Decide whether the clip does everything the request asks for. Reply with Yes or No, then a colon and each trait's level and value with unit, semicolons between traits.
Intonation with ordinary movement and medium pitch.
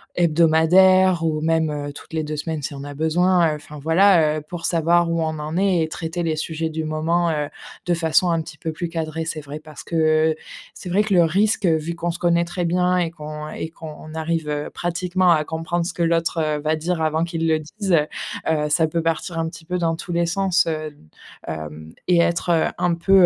No: narrow, 1.8 semitones; medium, 165 Hz